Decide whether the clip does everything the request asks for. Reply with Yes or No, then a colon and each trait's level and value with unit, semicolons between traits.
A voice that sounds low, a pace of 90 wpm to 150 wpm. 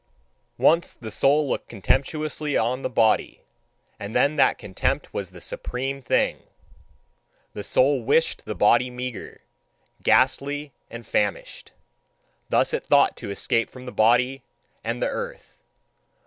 Yes: low, 125 Hz; slow, 135 wpm